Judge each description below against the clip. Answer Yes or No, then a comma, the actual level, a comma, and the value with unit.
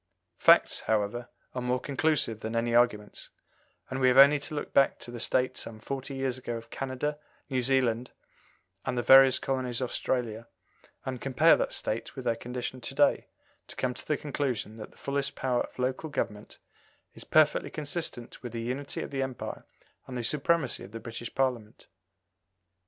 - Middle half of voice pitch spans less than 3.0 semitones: Yes, narrow, 2.5 semitones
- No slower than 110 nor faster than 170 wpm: No, average, 180 wpm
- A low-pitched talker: Yes, low, 125 Hz